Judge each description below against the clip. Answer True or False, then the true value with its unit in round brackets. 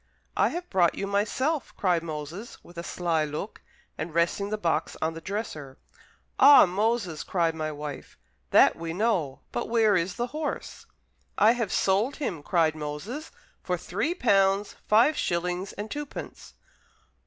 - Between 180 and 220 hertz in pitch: True (190 Hz)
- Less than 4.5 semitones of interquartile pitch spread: False (5.3 semitones)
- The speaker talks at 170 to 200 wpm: False (155 wpm)